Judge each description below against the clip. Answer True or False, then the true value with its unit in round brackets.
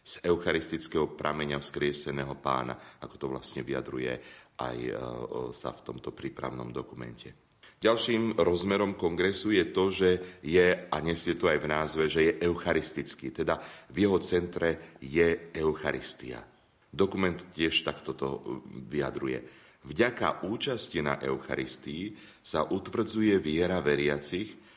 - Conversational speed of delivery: True (120 wpm)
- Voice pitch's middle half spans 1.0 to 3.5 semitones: False (5.1 semitones)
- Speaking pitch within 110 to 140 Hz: False (75 Hz)